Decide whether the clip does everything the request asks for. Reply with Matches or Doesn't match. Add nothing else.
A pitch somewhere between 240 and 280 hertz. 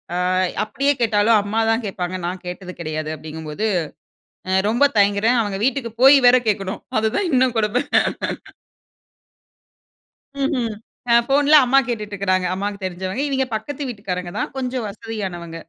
Doesn't match